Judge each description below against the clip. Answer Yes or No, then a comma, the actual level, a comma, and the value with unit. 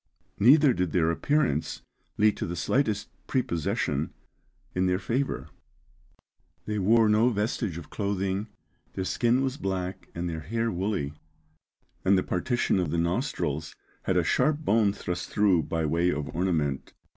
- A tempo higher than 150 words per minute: No, average, 145 wpm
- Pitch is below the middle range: Yes, very low, 95 Hz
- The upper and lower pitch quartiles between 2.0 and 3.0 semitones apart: No, average, 4.9 semitones